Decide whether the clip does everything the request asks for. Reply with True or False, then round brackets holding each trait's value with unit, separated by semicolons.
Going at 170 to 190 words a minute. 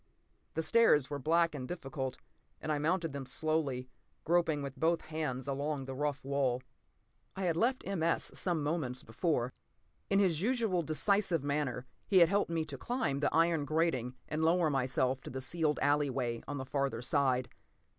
True (180 wpm)